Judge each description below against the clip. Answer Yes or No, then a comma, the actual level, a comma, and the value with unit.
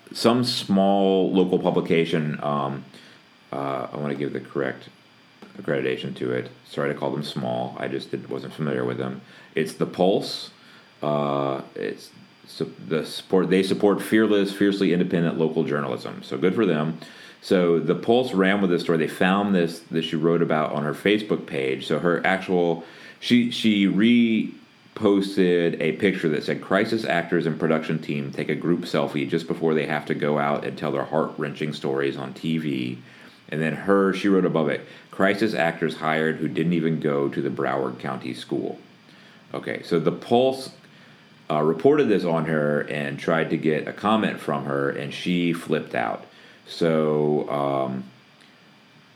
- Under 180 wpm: Yes, average, 170 wpm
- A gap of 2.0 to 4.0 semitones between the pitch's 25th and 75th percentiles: No, average, 4.4 semitones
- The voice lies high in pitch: No, very low, 80 Hz